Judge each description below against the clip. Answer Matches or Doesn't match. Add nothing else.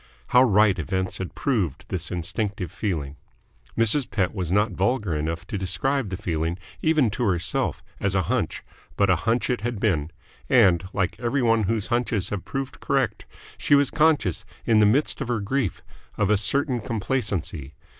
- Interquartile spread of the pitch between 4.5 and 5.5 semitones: Matches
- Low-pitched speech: Matches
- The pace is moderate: Matches